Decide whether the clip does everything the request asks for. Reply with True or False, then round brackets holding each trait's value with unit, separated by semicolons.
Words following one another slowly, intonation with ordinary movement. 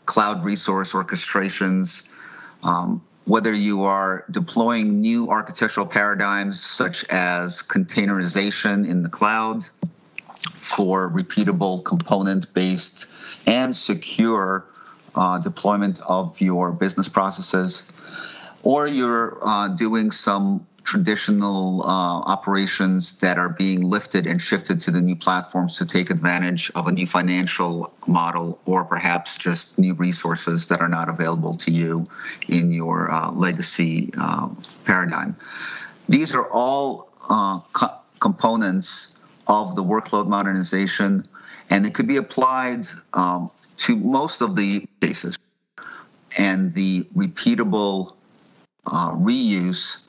True (115 wpm; 3.1 semitones)